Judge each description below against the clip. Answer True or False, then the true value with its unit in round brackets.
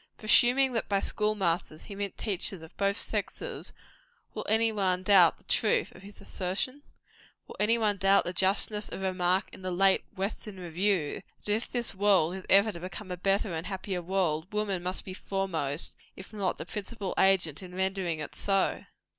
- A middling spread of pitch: False (2.3 semitones)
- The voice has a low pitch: False (195 Hz)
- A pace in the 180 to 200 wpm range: True (190 wpm)